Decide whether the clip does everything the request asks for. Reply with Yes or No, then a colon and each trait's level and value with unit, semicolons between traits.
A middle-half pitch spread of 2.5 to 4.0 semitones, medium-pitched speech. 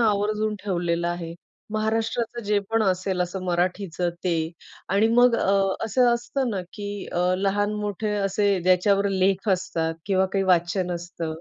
No: average, 2.8 semitones; high, 195 Hz